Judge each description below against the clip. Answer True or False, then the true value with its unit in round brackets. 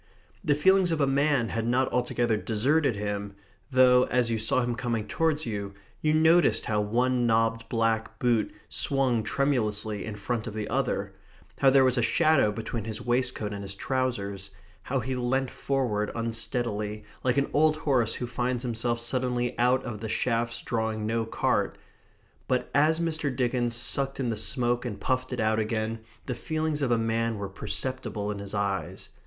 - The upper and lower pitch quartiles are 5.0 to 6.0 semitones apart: False (3.1 semitones)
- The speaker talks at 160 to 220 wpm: True (175 wpm)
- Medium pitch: False (120 Hz)